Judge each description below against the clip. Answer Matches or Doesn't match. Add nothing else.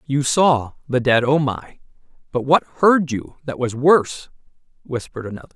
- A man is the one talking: Matches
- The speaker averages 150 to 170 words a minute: Matches